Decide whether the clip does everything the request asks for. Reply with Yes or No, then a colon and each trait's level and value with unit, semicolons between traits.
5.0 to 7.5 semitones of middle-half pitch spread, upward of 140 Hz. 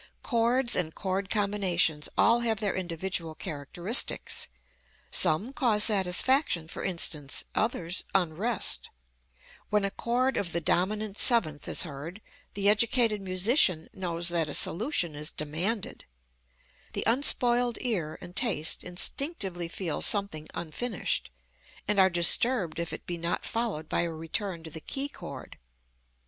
Yes: average, 5.3 semitones; high, 190 Hz